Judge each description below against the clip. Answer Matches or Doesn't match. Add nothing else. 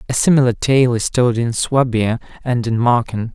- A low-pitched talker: Matches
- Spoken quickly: Doesn't match